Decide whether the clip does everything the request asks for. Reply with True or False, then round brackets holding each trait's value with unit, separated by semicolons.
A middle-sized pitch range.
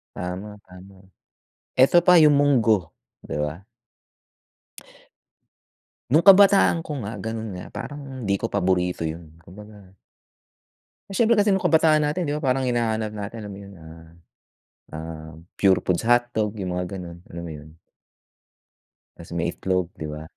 False (7.2 semitones)